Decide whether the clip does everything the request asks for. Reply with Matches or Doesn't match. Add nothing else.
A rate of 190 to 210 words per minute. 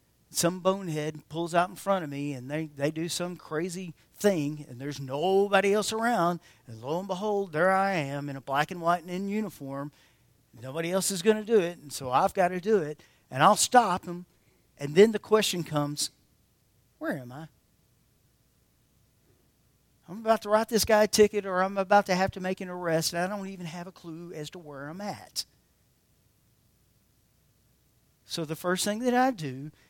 Matches